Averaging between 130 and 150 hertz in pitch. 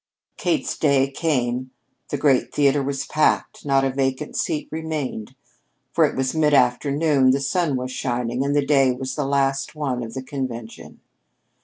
Yes: low, 135 Hz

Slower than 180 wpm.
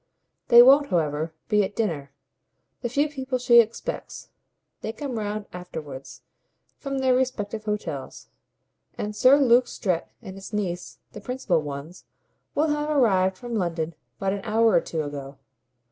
Yes: average, 150 wpm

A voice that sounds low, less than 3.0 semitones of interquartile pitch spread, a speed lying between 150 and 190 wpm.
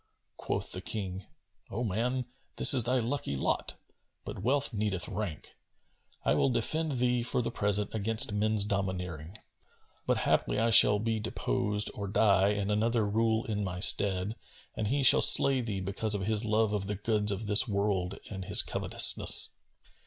Yes: low, 105 Hz; narrow, 2.5 semitones; average, 165 wpm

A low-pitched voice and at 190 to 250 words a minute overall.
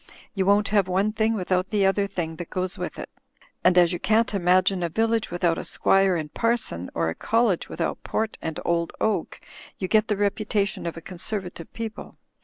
No: high, 195 Hz; fast, 205 wpm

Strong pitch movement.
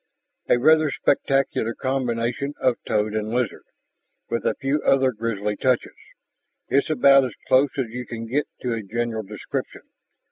No: average, 3.1 semitones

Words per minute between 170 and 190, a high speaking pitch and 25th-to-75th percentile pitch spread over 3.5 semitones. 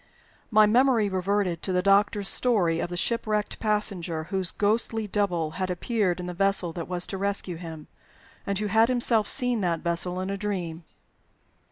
No: average, 175 wpm; high, 195 Hz; average, 3.1 semitones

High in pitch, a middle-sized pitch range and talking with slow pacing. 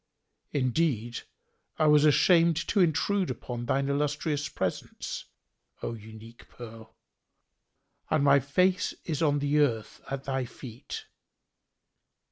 No: medium, 140 Hz; average, 4.3 semitones; slow, 110 wpm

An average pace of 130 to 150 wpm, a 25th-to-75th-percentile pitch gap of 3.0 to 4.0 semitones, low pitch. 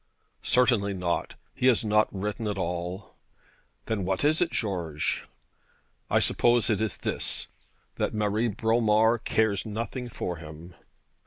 Yes: slow, 135 wpm; average, 3.4 semitones; low, 105 Hz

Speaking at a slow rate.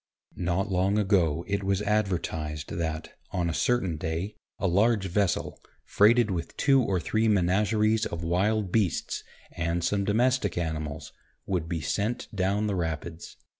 No: average, 145 wpm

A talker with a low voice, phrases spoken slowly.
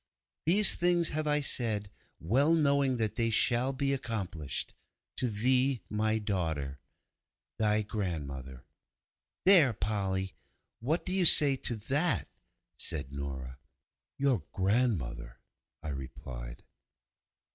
Yes: low, 110 Hz; slow, 110 wpm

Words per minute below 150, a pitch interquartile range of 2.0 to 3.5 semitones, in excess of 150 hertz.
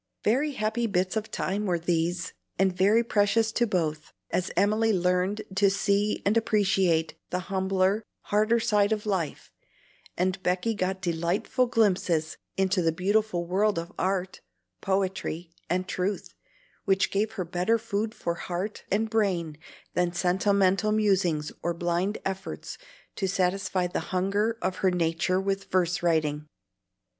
Yes: average, 140 wpm; average, 2.8 semitones; high, 190 Hz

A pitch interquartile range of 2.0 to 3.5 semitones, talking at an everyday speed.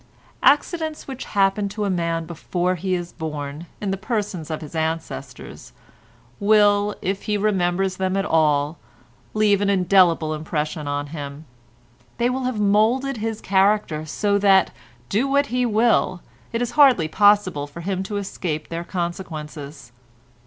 No: average, 4.5 semitones; average, 150 wpm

